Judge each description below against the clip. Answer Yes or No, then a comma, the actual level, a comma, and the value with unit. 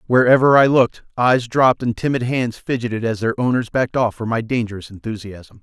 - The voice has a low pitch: Yes, low, 120 Hz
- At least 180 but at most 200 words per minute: Yes, average, 190 wpm